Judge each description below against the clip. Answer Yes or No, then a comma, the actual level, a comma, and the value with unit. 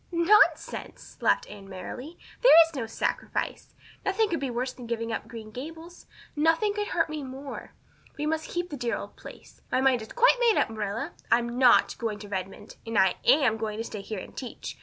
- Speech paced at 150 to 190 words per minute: No, average, 200 wpm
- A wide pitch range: Yes, wide, 6.5 semitones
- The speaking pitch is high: Yes, very high, 255 Hz